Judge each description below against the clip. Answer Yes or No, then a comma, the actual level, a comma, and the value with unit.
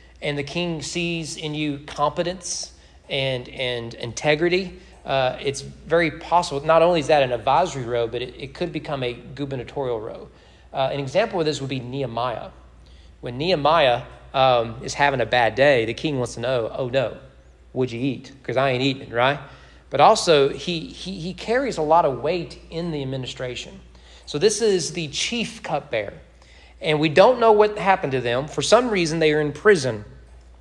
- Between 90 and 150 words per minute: No, average, 185 wpm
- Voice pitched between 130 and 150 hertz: Yes, medium, 140 Hz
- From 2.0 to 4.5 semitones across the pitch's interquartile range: No, average, 5.3 semitones